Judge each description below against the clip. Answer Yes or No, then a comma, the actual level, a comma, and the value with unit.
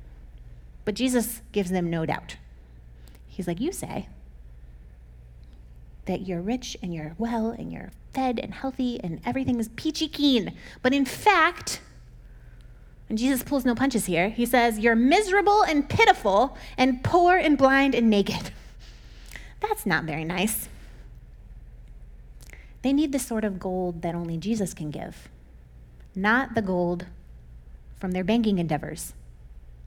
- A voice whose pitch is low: No, medium, 185 Hz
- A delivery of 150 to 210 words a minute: No, average, 140 wpm